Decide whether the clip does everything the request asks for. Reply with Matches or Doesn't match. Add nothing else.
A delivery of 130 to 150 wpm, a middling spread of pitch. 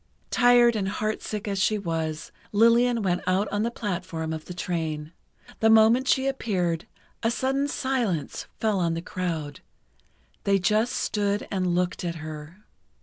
Matches